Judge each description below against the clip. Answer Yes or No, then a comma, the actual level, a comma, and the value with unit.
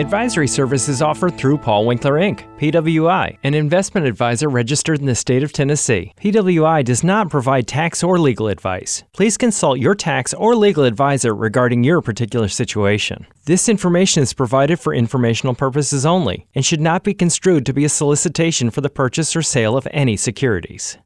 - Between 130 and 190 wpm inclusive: Yes, average, 175 wpm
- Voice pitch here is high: No, medium, 140 Hz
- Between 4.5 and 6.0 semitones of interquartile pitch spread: Yes, wide, 5.4 semitones